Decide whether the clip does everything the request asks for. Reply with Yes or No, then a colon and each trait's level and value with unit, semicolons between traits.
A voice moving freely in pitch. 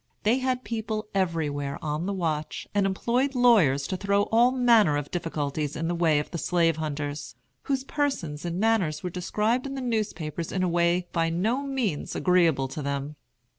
Yes: wide, 6.7 semitones